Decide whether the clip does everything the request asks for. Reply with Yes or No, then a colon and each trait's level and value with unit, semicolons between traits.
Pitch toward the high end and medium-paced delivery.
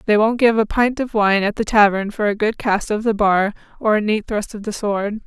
No: high, 215 Hz; fast, 275 wpm